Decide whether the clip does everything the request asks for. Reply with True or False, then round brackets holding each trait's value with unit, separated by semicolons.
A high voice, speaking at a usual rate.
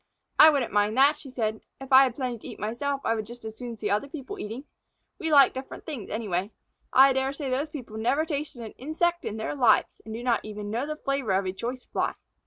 False (255 Hz; 240 wpm)